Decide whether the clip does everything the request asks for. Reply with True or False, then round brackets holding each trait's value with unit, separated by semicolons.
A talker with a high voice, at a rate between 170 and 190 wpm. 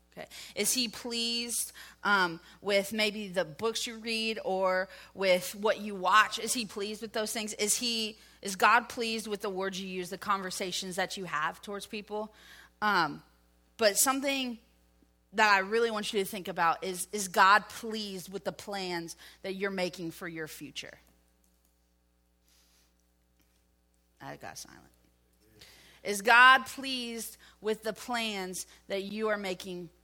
False (195 Hz; 150 wpm)